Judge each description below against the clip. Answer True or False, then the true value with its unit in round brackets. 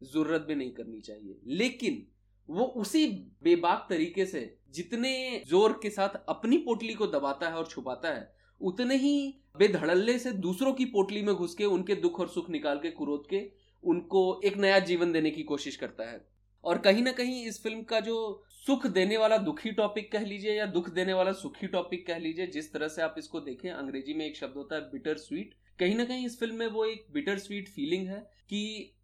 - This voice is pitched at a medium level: False (195 Hz)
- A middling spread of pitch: False (6.2 semitones)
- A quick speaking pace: True (205 wpm)